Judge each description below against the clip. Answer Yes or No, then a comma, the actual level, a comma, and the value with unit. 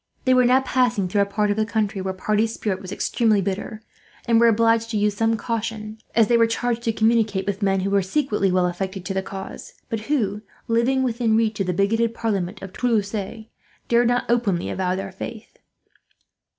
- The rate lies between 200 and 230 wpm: Yes, fast, 205 wpm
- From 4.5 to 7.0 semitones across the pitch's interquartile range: No, average, 2.9 semitones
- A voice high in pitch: Yes, high, 215 Hz